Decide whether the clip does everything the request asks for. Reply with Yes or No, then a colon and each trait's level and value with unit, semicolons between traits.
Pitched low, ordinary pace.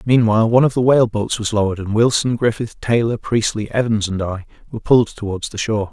No: low, 110 Hz; fast, 215 wpm